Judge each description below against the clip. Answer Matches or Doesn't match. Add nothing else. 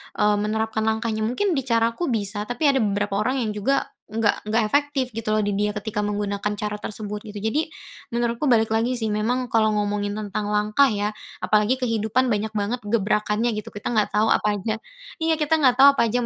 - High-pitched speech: Matches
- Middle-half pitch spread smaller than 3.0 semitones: Matches